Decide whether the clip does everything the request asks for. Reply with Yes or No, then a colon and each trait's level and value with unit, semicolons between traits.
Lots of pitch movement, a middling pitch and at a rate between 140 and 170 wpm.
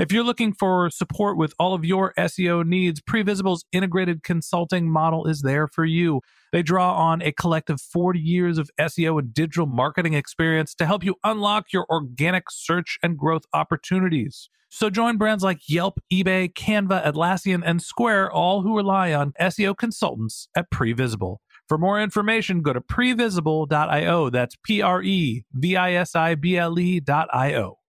No: average, 3.2 semitones; medium, 175 Hz; average, 165 wpm